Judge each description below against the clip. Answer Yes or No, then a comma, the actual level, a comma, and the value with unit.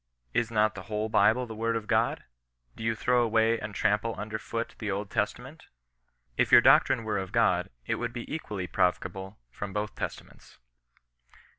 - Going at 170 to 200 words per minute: Yes, average, 185 wpm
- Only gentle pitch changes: Yes, narrow, 2.0 semitones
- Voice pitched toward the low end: Yes, low, 110 Hz